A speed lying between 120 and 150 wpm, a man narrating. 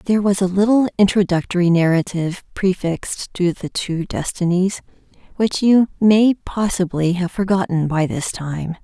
No: slow, 135 wpm; female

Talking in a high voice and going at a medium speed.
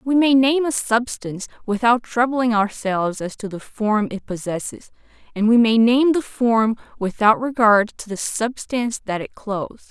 Yes: high, 225 Hz; average, 170 wpm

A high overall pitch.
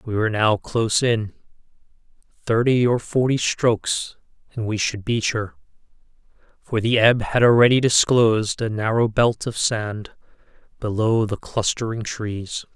No: low, 110 Hz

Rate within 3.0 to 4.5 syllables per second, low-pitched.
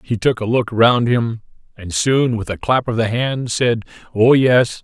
Yes: 4.2 syllables/s; low, 115 Hz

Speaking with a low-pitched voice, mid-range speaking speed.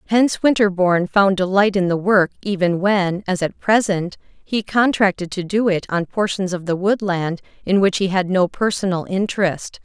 No: high, 190 Hz; average, 175 wpm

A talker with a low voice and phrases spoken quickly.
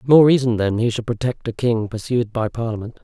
Yes: low, 115 Hz; fast, 215 wpm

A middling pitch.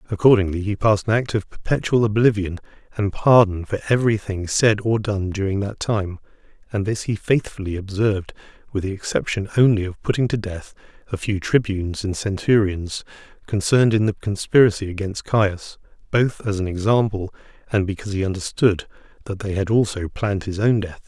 No: low, 100 Hz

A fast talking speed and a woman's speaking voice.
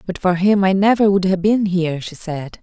Yes: fast, 250 wpm; female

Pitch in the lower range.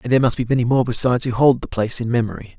Yes: low, 120 Hz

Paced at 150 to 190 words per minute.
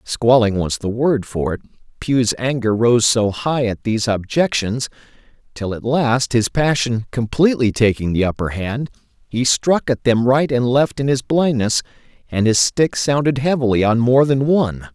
Yes: average, 175 wpm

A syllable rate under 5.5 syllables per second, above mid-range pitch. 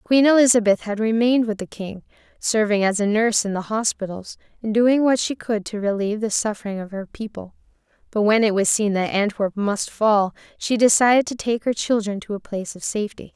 No: 5.6 syllables/s; high, 215 Hz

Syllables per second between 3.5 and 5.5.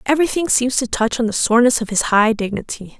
No: 6.3 syllables/s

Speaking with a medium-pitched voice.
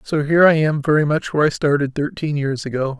Yes: medium, 150 Hz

